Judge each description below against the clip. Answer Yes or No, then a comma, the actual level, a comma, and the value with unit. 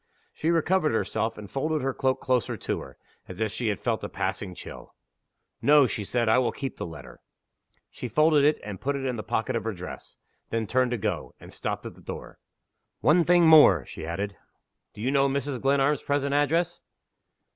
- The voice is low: Yes, low, 130 Hz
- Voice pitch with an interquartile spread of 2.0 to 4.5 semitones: No, average, 5.0 semitones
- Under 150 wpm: No, average, 200 wpm